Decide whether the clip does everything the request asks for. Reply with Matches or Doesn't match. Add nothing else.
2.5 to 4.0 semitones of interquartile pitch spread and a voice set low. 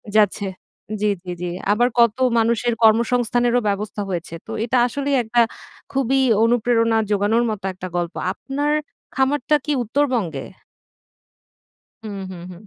Doesn't match